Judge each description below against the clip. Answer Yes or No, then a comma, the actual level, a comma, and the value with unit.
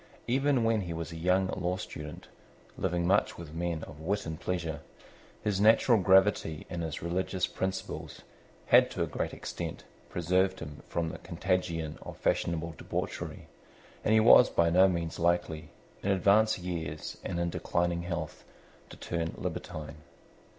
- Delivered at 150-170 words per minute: Yes, average, 155 wpm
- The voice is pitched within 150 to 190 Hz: No, very low, 85 Hz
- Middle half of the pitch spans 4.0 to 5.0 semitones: No, narrow, 2.6 semitones